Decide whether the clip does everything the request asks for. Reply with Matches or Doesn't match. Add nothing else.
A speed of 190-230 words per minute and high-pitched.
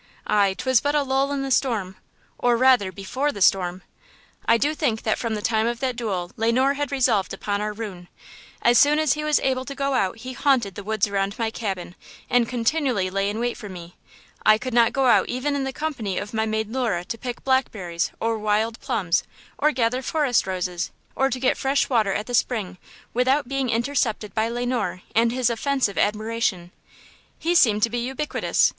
Matches